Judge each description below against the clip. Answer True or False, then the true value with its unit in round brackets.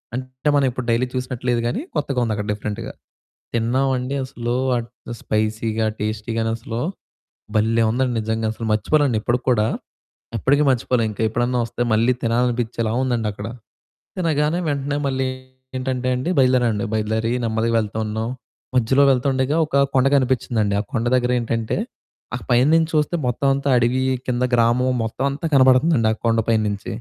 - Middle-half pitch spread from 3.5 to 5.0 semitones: False (2.7 semitones)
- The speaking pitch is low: True (120 Hz)